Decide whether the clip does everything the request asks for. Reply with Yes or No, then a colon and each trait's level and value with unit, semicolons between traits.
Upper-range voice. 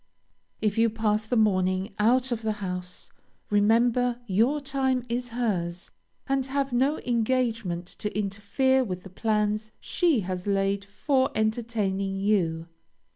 Yes: high, 215 Hz